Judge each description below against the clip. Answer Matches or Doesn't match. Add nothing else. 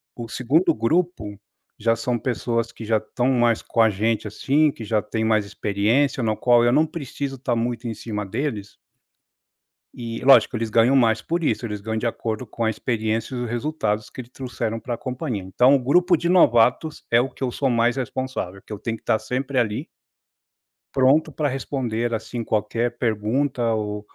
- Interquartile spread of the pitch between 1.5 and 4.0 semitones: Matches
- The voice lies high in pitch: Doesn't match